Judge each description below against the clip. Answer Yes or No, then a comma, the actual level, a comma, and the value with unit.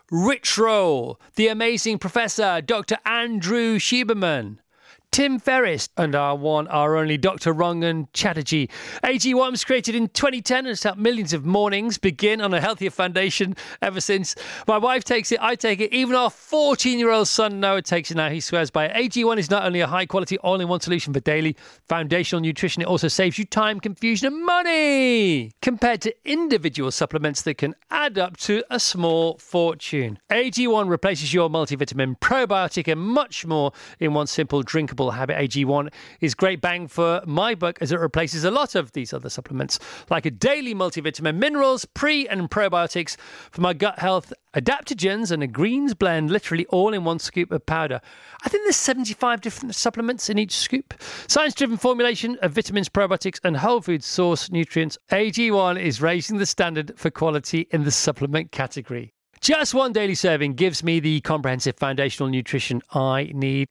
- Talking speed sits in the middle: Yes, average, 175 wpm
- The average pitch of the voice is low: No, medium, 185 Hz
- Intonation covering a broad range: Yes, wide, 6.2 semitones